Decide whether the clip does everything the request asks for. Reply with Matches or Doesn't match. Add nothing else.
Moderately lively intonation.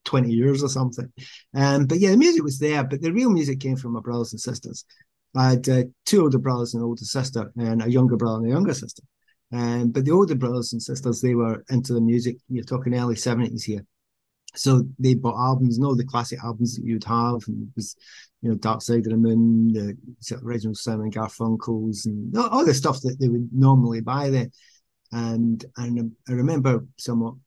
Doesn't match